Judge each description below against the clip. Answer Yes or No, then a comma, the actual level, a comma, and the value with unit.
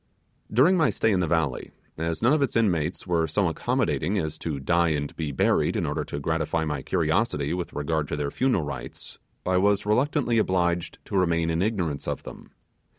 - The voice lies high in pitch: No, very low, 85 Hz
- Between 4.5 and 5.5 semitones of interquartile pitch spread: Yes, average, 4.9 semitones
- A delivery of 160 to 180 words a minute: No, average, 195 wpm